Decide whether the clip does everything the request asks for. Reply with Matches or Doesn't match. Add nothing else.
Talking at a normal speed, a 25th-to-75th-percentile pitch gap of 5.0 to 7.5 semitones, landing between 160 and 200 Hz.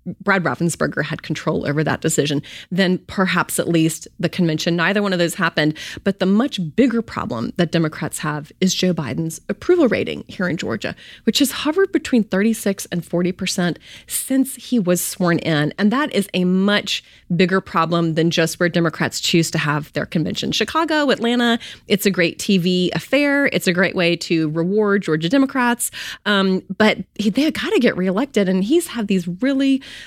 Matches